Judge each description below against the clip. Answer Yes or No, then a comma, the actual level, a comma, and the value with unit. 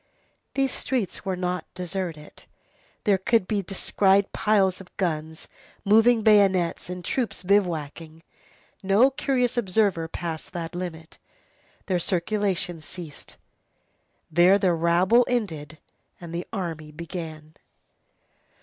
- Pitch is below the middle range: No, medium, 180 Hz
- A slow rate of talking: Yes, slow, 110 wpm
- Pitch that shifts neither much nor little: Yes, average, 3.5 semitones